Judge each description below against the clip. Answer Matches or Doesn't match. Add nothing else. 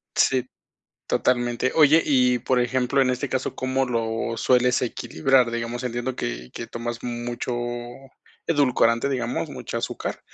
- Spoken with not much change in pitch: Matches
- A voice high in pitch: Doesn't match